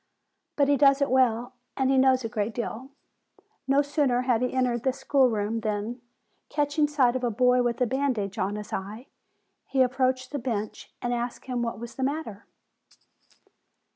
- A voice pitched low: No, very high, 250 Hz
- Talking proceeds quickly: No, average, 180 wpm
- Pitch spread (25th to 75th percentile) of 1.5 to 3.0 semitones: Yes, narrow, 2.6 semitones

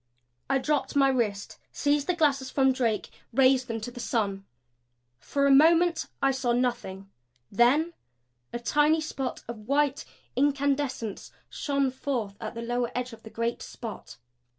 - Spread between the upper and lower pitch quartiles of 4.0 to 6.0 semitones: No, average, 3.4 semitones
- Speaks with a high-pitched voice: Yes, very high, 260 Hz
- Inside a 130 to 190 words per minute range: Yes, average, 150 wpm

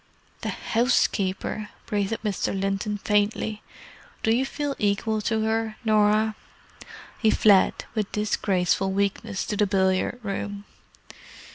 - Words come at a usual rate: No, slow, 115 wpm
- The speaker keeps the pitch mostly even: Yes, narrow, 1.8 semitones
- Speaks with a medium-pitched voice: No, high, 210 Hz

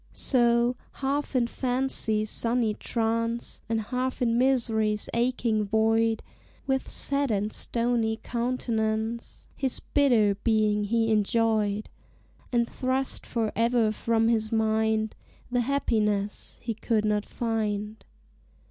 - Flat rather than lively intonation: Yes, narrow, 2.1 semitones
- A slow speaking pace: Yes, slow, 110 wpm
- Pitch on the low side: No, high, 230 Hz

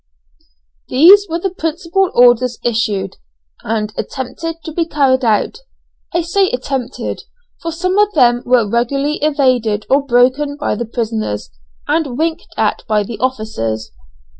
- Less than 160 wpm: Yes, average, 140 wpm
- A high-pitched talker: Yes, very high, 260 Hz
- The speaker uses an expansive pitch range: Yes, wide, 6.0 semitones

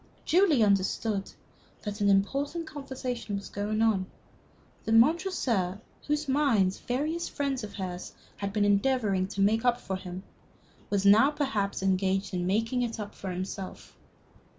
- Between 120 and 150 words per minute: Yes, average, 145 wpm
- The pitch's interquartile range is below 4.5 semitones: No, average, 5.2 semitones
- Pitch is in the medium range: No, high, 210 Hz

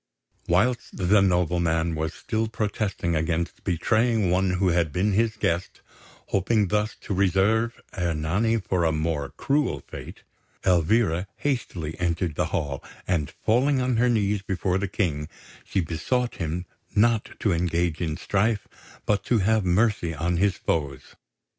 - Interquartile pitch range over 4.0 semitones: Yes, average, 4.5 semitones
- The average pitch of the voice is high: No, very low, 95 Hz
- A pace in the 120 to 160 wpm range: Yes, average, 145 wpm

